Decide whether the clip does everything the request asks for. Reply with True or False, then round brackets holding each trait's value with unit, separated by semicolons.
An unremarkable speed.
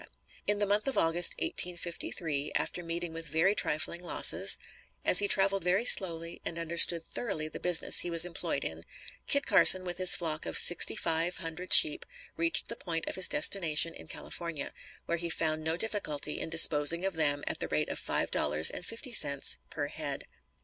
True (185 wpm)